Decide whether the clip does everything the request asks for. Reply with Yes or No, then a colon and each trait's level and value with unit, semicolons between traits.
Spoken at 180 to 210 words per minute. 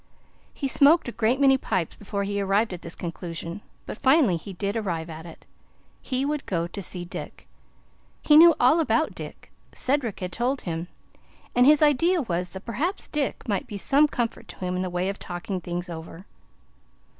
Yes: average, 190 wpm